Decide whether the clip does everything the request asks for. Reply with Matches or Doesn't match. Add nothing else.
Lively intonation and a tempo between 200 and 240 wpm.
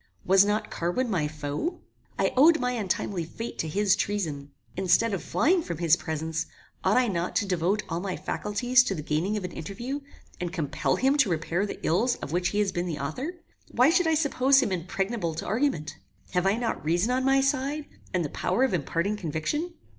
Matches